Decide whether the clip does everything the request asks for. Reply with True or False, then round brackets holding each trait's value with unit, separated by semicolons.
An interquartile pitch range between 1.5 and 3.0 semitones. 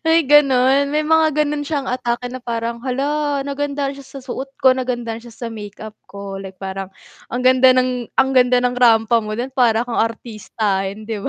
False (3.4 semitones)